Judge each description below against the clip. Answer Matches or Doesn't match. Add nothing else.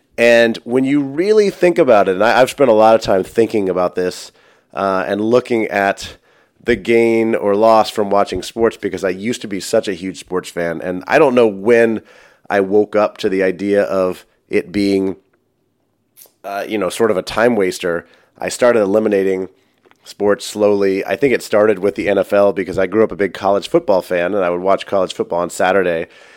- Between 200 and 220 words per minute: Matches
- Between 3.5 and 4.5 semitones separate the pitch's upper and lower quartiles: Doesn't match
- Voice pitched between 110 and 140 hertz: Doesn't match